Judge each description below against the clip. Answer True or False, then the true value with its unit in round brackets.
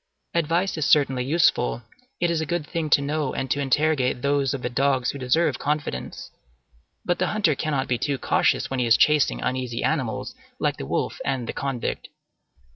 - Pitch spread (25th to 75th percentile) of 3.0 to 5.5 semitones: True (3.4 semitones)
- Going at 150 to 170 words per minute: False (190 wpm)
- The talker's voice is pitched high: False (140 Hz)